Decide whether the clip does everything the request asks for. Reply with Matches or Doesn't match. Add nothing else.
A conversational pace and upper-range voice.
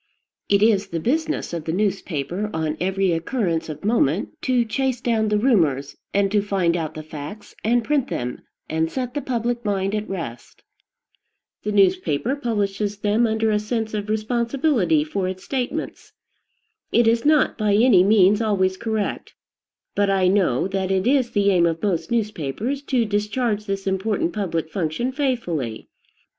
Matches